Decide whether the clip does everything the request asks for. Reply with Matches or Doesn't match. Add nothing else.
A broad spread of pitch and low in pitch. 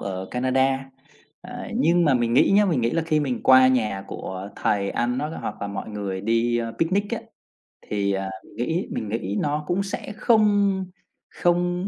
Matches